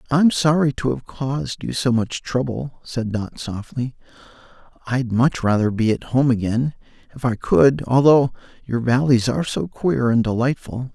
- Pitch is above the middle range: No, low, 125 Hz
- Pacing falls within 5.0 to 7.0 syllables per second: No, 4.5 syllables/s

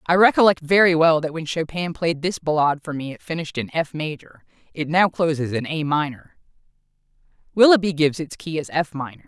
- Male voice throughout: No, female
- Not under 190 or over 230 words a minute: Yes, average, 195 wpm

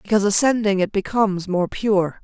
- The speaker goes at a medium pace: Yes, average, 160 wpm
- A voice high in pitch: Yes, high, 200 Hz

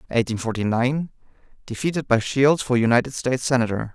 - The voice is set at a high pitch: No, low, 125 Hz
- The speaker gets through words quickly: No, slow, 135 wpm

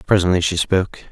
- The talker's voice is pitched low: Yes, very low, 90 Hz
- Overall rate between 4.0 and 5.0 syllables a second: No, 6.5 syllables/s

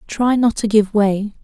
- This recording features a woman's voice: Yes, female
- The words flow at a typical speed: No, fast, 210 wpm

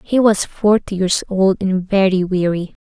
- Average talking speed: Yes, average, 170 wpm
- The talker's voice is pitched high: Yes, high, 195 Hz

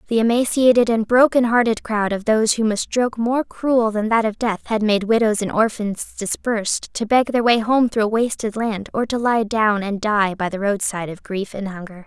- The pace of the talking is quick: Yes, fast, 220 wpm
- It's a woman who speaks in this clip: Yes, female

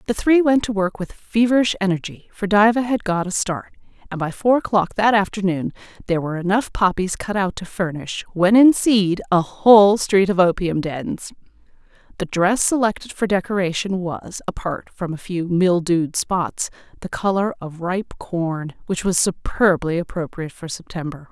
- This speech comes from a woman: Yes, female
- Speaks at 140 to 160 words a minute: No, average, 170 wpm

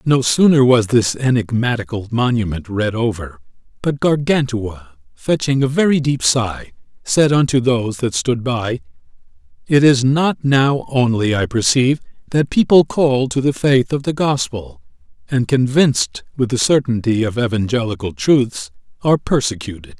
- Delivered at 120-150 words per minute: Yes, average, 140 wpm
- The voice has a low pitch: Yes, low, 120 Hz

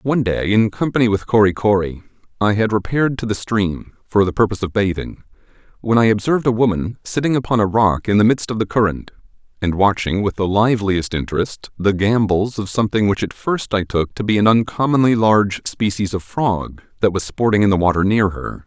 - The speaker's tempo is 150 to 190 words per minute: No, fast, 205 wpm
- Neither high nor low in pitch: No, low, 105 Hz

